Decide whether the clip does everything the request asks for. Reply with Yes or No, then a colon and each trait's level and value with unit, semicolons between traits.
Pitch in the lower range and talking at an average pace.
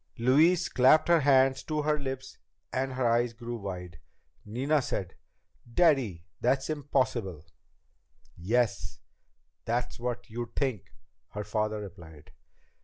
No: low, 120 Hz; slow, 115 wpm